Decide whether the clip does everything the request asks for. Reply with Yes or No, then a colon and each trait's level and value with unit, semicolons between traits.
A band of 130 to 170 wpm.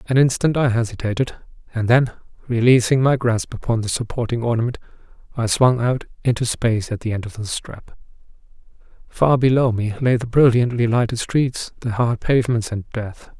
Yes: average, 165 wpm